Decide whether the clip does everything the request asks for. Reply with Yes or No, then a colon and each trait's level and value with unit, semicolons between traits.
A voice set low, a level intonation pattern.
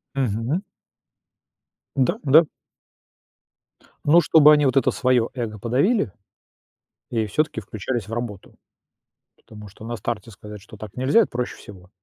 No: low, 120 Hz; average, 4.4 semitones